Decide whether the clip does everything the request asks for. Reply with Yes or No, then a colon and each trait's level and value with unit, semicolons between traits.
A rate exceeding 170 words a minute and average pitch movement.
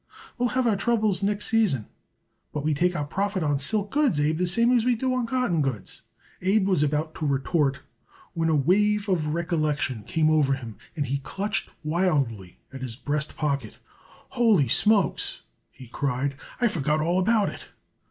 No: average, 180 wpm; wide, 6.6 semitones